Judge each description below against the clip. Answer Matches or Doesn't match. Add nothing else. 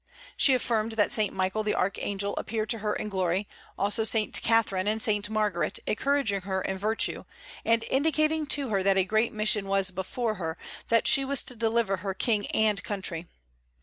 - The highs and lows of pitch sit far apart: Doesn't match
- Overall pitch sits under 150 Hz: Doesn't match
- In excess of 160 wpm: Matches